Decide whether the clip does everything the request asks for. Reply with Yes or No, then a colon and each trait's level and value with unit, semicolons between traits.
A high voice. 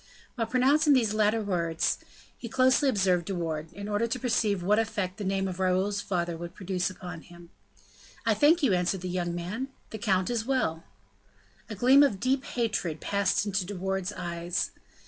Yes: high, 195 Hz